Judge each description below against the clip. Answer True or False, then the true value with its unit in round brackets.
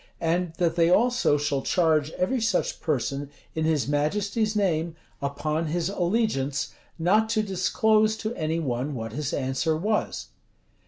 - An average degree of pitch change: False (5.9 semitones)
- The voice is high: False (165 Hz)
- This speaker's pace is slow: False (145 wpm)